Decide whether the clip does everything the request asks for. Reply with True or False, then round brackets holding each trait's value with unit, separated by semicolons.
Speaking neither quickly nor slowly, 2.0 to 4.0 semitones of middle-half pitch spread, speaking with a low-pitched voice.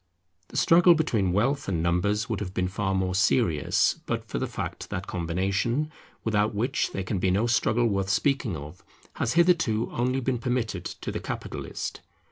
False (175 wpm; 4.7 semitones; 105 Hz)